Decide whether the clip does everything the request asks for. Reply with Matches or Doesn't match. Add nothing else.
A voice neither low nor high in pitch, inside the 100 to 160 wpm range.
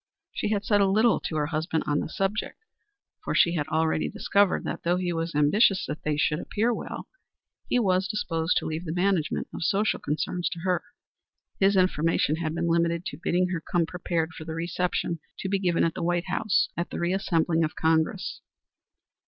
Doesn't match